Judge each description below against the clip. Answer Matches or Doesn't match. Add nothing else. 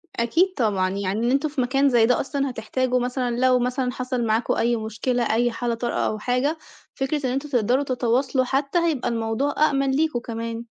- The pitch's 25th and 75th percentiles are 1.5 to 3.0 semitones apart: Matches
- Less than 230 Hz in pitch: Doesn't match